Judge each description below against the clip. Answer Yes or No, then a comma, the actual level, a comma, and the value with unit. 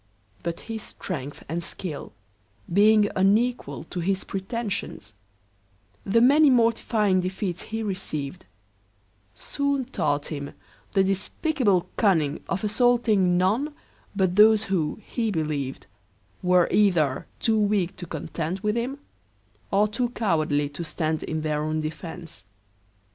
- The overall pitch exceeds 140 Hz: Yes, high, 190 Hz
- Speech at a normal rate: No, slow, 120 wpm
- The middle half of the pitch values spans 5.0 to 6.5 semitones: Yes, wide, 5.6 semitones